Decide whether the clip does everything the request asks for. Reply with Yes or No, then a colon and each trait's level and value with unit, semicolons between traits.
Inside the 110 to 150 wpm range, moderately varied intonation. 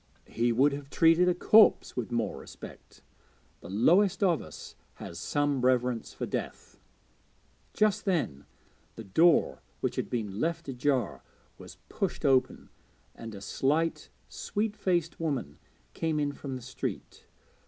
No: average, 140 wpm; wide, 5.9 semitones